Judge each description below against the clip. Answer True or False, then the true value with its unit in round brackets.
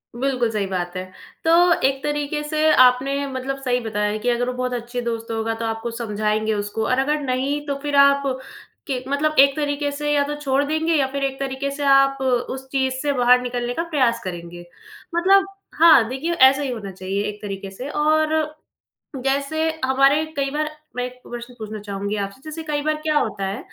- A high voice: True (265 Hz)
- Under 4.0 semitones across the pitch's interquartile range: False (4.3 semitones)